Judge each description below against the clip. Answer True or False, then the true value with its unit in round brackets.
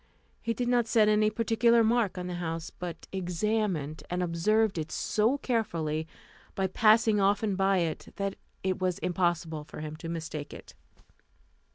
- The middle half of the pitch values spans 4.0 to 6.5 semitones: True (4.6 semitones)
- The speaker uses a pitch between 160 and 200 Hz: True (190 Hz)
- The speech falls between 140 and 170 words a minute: True (160 wpm)